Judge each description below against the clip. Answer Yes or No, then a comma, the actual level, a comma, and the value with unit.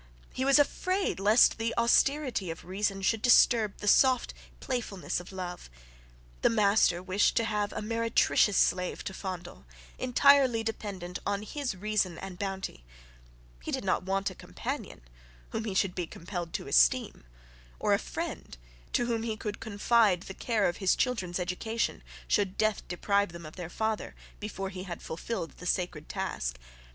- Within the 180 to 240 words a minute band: No, average, 165 wpm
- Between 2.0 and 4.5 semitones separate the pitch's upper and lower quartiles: Yes, average, 3.9 semitones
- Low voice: No, high, 200 Hz